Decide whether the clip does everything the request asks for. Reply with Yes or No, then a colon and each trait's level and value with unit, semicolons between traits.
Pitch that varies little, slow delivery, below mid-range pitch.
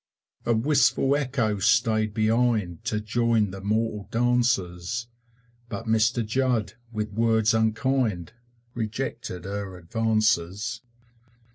Yes: narrow, 2.3 semitones; slow, 100 wpm; low, 110 Hz